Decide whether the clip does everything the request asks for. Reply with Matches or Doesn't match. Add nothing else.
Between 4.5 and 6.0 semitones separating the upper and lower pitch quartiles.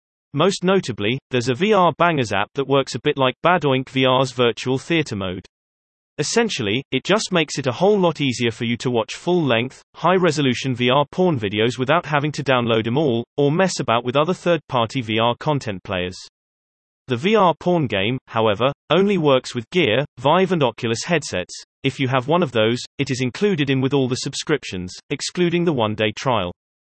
Matches